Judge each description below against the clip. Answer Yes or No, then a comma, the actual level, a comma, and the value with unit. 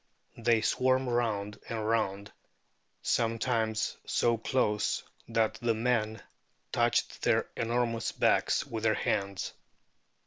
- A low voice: Yes, low, 115 Hz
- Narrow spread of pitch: Yes, narrow, 1.5 semitones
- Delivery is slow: Yes, slow, 105 wpm